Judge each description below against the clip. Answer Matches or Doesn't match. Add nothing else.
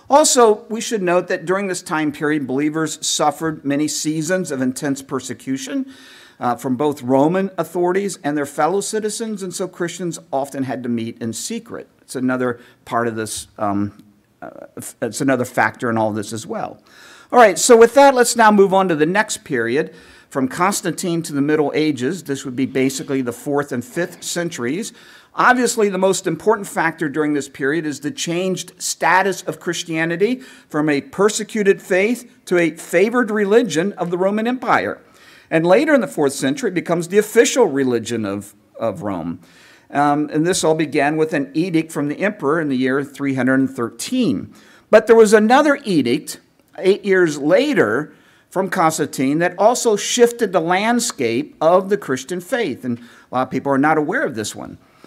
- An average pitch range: Doesn't match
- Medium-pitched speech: Matches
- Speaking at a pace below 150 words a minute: Doesn't match